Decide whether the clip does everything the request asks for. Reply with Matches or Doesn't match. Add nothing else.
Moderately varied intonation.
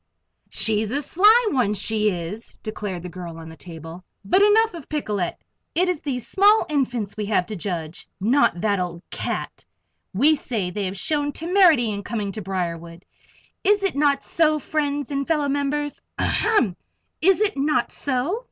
Doesn't match